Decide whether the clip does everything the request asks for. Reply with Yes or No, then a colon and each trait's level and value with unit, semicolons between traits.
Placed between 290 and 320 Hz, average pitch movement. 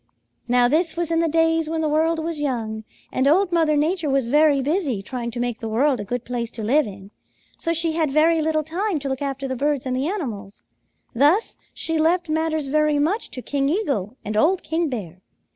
Yes: very high, 295 Hz; average, 4.7 semitones